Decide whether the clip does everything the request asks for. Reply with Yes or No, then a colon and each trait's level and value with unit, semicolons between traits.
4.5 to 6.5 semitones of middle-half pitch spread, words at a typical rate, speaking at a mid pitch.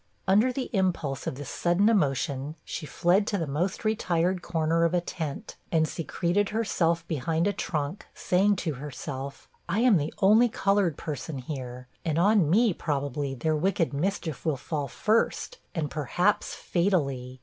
Yes: average, 5.2 semitones; average, 160 wpm; medium, 165 Hz